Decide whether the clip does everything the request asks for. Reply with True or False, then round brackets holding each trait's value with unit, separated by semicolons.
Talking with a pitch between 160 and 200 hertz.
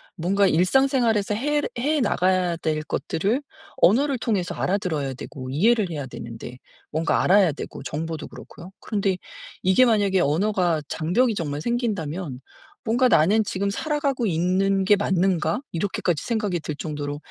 True (185 Hz)